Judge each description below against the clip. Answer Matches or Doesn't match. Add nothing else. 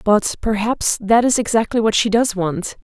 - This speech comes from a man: Doesn't match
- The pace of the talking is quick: Doesn't match